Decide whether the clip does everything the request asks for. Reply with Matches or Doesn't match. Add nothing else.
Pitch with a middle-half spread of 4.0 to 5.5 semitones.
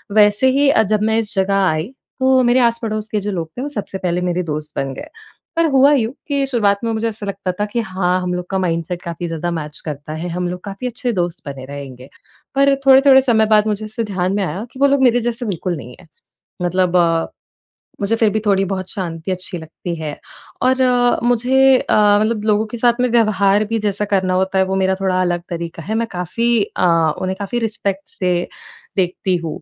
Matches